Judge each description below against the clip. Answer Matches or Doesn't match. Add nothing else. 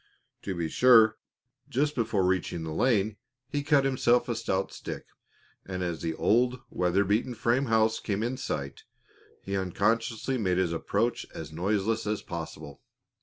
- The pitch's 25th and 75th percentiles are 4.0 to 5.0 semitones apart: Matches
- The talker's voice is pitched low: Matches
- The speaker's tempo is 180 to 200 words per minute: Doesn't match